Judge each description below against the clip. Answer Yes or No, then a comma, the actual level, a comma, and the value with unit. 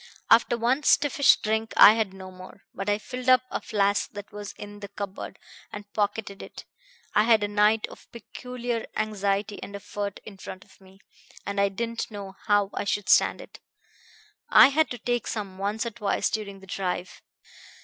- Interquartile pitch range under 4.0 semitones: Yes, narrow, 2.4 semitones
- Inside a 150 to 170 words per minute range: No, average, 185 wpm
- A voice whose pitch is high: Yes, high, 205 Hz